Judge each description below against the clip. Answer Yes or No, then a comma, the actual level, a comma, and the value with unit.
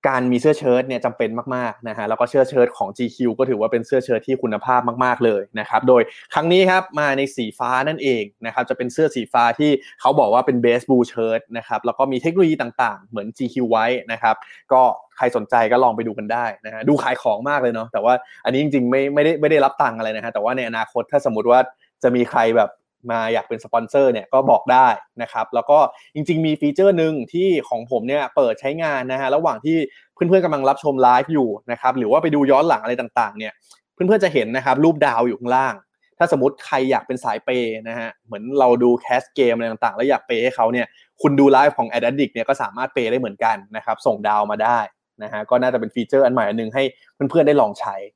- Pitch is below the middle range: Yes, low, 125 Hz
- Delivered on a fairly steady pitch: No, average, 3.6 semitones